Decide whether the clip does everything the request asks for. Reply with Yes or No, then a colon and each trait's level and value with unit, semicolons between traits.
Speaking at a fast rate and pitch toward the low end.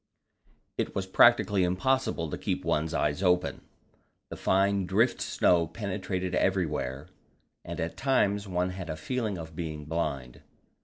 No: average, 140 wpm; very low, 90 Hz